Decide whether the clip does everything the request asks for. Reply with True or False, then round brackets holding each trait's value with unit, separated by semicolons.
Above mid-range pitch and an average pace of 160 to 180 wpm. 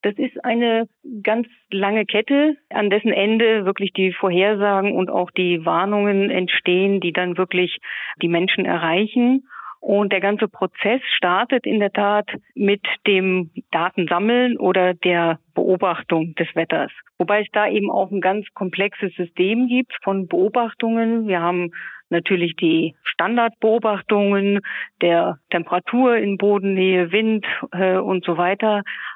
False (200 Hz; 130 wpm)